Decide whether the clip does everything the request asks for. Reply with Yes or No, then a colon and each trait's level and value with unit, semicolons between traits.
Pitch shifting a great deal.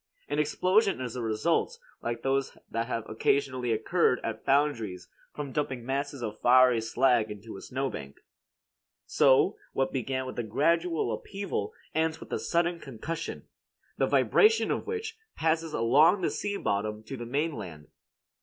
Yes: wide, 6.0 semitones